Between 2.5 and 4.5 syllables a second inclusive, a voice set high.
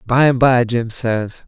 No: 3.7 syllables/s; low, 120 Hz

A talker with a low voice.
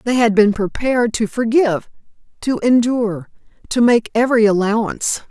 No: high, 225 Hz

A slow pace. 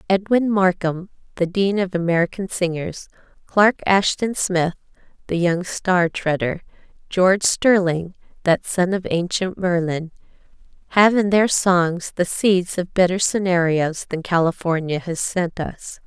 Yes: slow, 130 wpm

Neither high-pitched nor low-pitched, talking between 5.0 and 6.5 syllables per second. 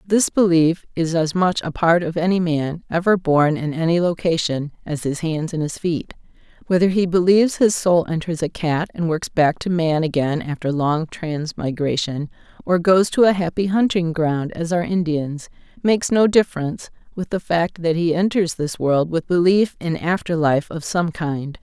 No: medium, 170 Hz; 4.7 syllables/s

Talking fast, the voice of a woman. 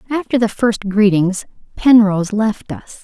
No: average, 140 wpm; female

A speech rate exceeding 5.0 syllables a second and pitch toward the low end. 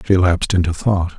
Yes: 5.9 syllables/s; very low, 90 Hz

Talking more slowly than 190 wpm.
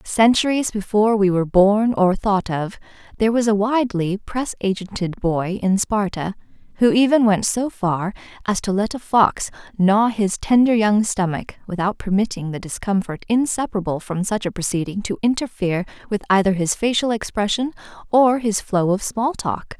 Yes: average, 165 wpm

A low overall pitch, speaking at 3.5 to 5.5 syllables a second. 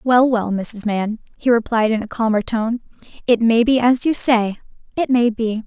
No: high, 230 Hz; 4.6 syllables/s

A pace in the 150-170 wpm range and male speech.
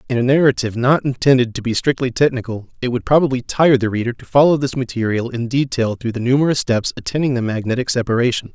No: fast, 205 wpm; male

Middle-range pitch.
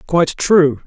Yes: medium, 155 Hz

